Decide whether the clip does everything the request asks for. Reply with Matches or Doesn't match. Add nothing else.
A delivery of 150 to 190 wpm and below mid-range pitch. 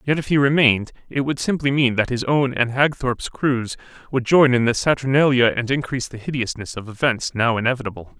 Doesn't match